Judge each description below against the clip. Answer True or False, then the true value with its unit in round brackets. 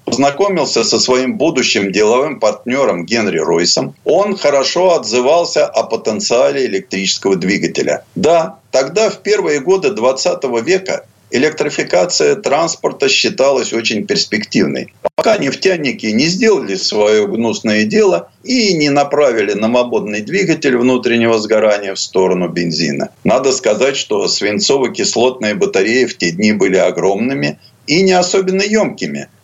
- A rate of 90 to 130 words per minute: True (120 wpm)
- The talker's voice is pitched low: True (130 Hz)